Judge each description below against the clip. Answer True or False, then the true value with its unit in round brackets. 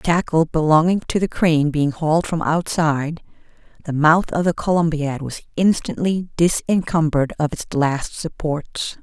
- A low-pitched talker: False (160 Hz)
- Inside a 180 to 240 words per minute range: False (145 wpm)